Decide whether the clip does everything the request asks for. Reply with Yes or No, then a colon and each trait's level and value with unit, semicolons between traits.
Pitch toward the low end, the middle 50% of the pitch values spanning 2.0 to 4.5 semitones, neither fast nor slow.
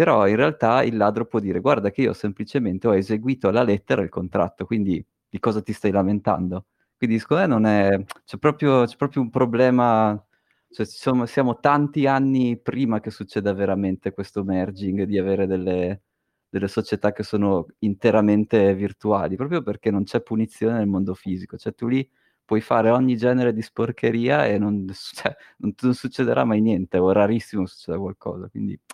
No: low, 105 Hz; average, 3.6 semitones; fast, 180 wpm